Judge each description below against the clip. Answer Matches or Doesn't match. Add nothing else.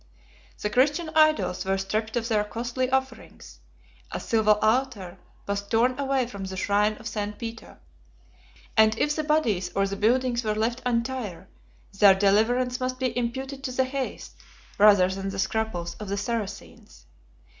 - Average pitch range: Matches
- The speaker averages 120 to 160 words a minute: Matches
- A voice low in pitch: Doesn't match